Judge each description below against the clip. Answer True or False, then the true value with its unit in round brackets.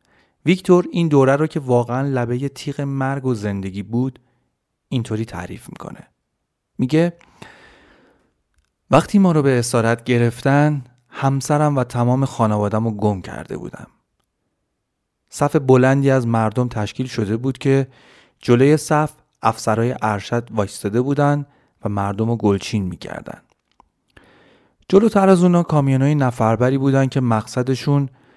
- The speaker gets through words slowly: False (120 wpm)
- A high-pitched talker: False (130 Hz)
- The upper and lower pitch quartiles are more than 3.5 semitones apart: True (3.9 semitones)